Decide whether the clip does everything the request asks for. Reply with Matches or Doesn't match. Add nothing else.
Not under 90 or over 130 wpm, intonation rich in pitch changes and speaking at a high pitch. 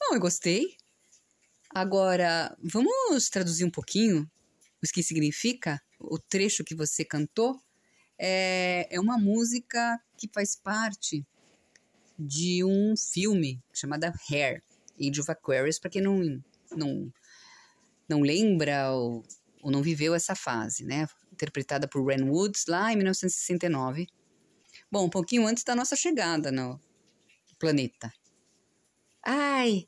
Doesn't match